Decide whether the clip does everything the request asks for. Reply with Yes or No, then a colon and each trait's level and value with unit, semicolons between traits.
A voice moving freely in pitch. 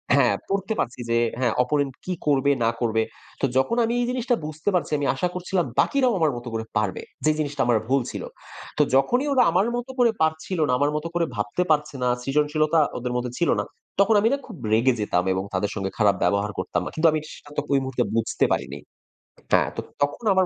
Yes: wide, 6.7 semitones